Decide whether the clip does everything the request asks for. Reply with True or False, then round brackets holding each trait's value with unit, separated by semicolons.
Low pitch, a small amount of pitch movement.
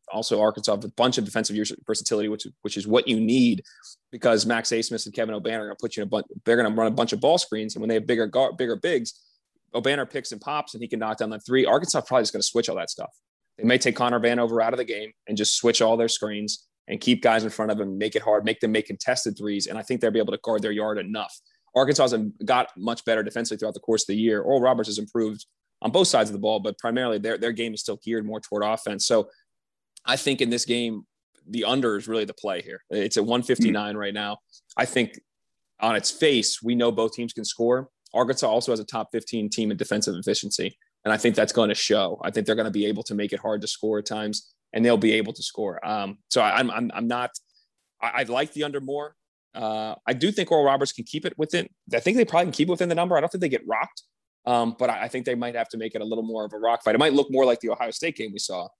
True (115 Hz; 2.3 semitones)